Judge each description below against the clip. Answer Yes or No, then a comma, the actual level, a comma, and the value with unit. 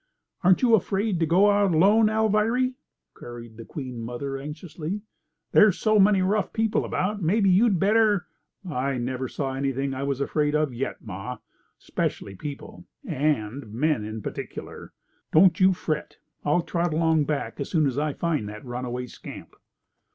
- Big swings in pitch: Yes, wide, 6.8 semitones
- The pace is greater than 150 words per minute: Yes, average, 160 wpm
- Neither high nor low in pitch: Yes, medium, 155 Hz